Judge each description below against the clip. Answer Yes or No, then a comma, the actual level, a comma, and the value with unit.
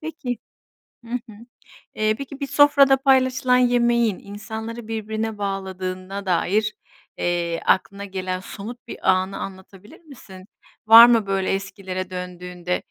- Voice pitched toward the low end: No, high, 205 Hz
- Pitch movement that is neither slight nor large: Yes, average, 4.2 semitones